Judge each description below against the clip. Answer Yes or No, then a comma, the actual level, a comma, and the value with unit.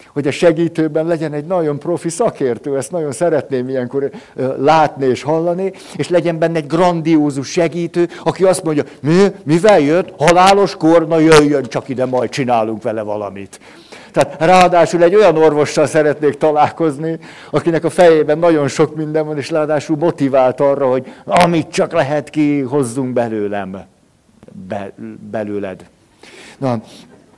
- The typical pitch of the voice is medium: Yes, medium, 155 Hz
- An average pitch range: Yes, average, 3.7 semitones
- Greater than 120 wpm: Yes, average, 140 wpm